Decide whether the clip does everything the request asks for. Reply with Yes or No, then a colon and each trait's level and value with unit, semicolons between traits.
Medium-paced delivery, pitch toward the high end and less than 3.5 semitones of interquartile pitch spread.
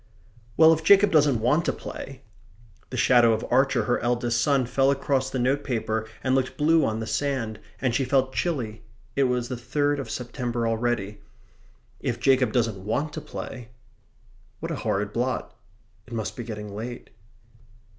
No: average, 165 wpm; low, 125 Hz; average, 3.1 semitones